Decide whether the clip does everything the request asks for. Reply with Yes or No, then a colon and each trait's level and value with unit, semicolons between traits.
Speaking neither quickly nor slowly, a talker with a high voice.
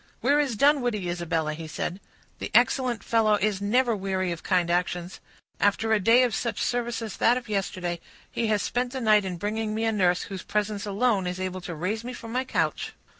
No: fast, 210 wpm; high, 210 Hz